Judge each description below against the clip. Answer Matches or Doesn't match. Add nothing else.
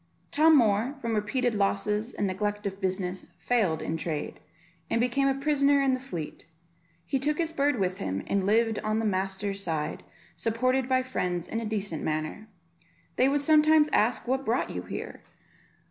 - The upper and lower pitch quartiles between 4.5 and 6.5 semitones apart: Matches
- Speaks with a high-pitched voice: Matches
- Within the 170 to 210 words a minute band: Matches